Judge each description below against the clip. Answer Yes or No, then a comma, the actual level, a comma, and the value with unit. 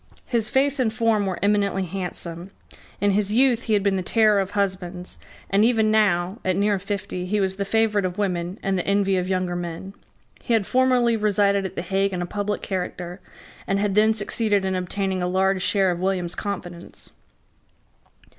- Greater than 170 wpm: Yes, average, 190 wpm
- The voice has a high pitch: Yes, high, 195 Hz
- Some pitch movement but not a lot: No, narrow, 2.3 semitones